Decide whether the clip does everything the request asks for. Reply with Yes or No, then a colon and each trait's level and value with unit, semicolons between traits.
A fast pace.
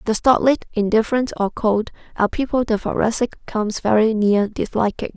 No: average, 150 wpm